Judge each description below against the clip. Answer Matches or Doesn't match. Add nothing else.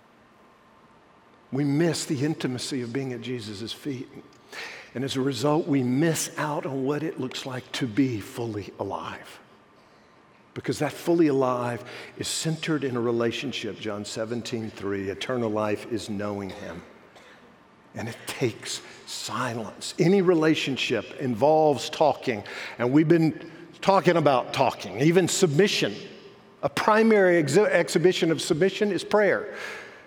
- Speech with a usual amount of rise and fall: Doesn't match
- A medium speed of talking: Doesn't match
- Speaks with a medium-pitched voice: Matches